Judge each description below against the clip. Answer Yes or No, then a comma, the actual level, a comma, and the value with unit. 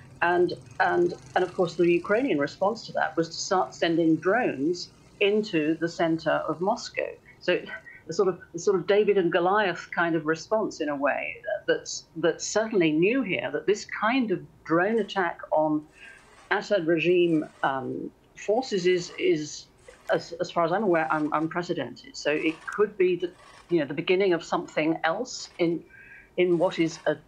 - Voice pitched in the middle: Yes, medium, 180 Hz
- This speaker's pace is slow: No, average, 175 wpm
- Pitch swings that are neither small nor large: Yes, average, 4.6 semitones